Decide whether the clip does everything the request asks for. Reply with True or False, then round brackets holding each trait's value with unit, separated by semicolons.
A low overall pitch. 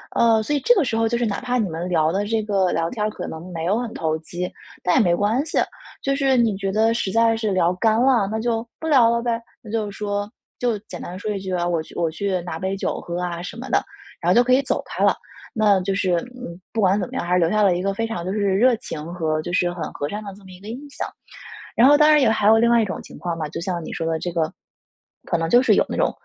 False (200 Hz)